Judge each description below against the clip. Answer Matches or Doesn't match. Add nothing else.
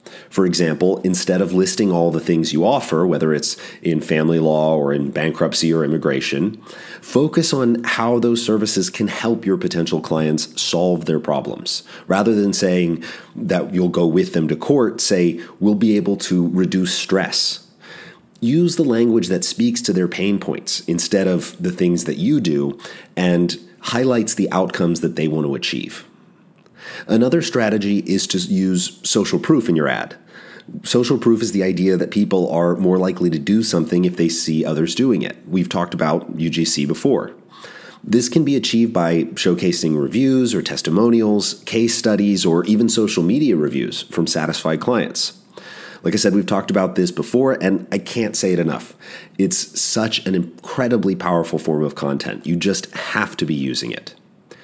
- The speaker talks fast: Doesn't match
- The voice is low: Matches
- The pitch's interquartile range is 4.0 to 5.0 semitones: Matches